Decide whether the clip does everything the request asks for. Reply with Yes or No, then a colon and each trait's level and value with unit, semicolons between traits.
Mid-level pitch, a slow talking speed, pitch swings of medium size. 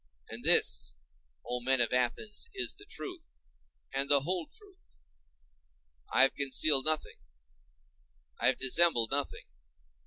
No: medium, 145 Hz; slow, 125 wpm; wide, 7.6 semitones